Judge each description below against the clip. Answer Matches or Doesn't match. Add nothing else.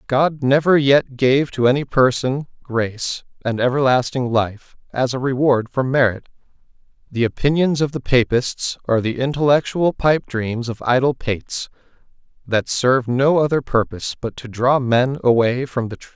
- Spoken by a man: Matches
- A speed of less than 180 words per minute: Matches